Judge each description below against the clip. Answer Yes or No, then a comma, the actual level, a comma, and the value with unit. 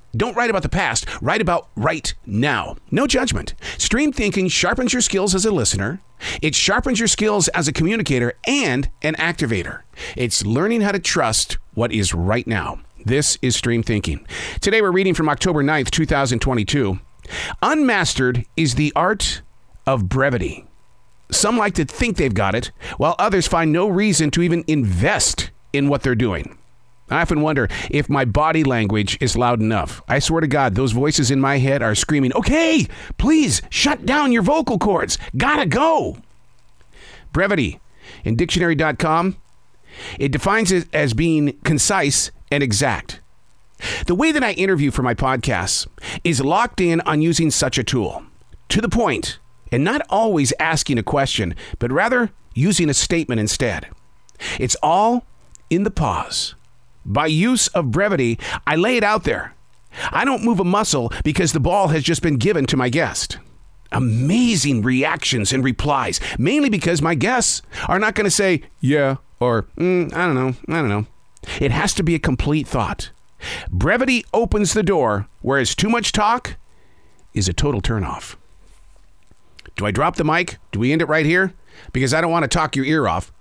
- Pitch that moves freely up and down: Yes, wide, 6.9 semitones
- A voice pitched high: No, medium, 145 Hz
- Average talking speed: Yes, average, 170 wpm